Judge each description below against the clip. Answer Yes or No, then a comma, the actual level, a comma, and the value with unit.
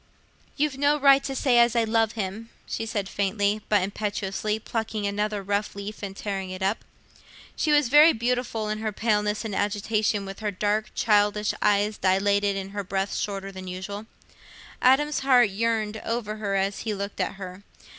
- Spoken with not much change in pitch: Yes, narrow, 2.1 semitones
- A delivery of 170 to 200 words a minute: Yes, average, 175 wpm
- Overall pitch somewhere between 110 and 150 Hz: No, high, 210 Hz